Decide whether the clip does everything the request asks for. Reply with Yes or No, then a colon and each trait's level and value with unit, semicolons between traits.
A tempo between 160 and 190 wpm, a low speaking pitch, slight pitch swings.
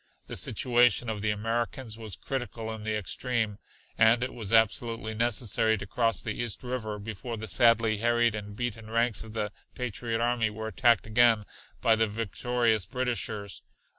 Yes: average, 165 wpm; low, 115 Hz; narrow, 1.8 semitones